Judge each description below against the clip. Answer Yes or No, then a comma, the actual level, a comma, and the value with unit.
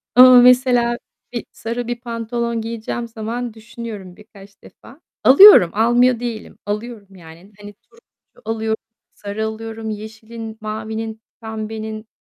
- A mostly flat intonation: Yes, narrow, 1.6 semitones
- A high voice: Yes, high, 225 Hz